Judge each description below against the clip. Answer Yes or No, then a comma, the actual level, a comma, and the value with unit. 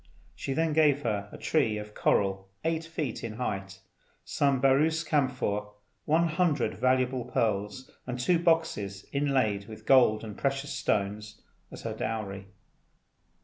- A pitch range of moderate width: No, wide, 5.8 semitones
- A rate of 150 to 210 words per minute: No, average, 140 wpm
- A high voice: No, low, 125 Hz